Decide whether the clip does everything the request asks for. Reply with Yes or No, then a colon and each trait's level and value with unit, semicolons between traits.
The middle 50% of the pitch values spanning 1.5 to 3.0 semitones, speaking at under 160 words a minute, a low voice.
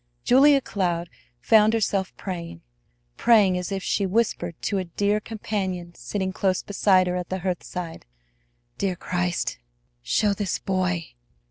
No: narrow, 2.6 semitones; slow, 135 wpm; medium, 185 Hz